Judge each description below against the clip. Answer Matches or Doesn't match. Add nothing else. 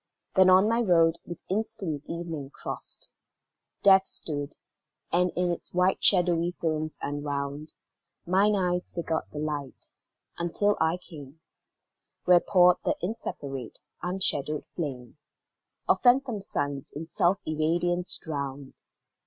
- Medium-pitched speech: Matches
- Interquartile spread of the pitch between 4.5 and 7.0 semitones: Doesn't match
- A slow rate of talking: Matches